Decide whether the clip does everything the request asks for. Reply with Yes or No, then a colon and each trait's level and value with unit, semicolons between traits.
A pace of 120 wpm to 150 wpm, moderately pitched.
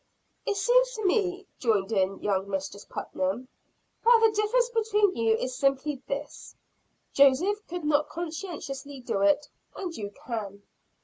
No: average, 140 wpm; very high, 290 Hz